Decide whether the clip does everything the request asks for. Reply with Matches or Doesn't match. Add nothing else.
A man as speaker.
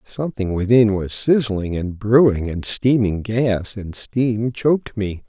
Matches